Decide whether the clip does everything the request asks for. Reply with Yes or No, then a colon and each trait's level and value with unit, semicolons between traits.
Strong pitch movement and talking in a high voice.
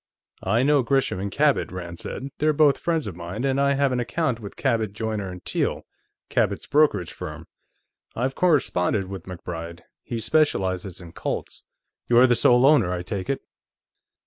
No: wide, 7.0 semitones; low, 115 Hz